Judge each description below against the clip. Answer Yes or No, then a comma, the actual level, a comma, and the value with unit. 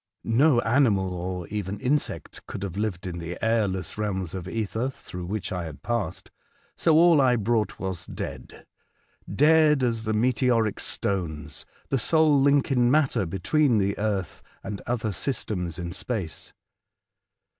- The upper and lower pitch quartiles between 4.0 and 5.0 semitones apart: No, wide, 5.4 semitones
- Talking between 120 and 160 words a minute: Yes, average, 150 wpm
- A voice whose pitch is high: No, low, 105 Hz